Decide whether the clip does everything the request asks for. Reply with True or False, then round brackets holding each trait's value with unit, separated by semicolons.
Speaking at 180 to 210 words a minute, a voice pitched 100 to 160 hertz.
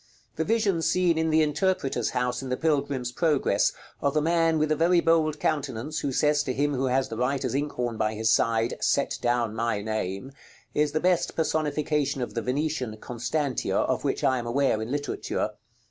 True (190 wpm; 140 Hz)